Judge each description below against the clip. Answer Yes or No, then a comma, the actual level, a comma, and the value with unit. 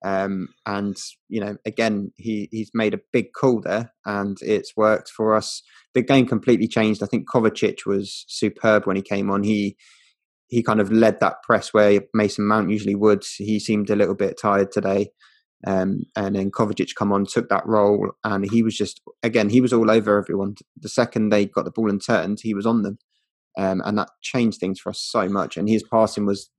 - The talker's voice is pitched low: Yes, low, 105 Hz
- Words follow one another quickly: Yes, fast, 210 wpm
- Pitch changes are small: Yes, narrow, 1.8 semitones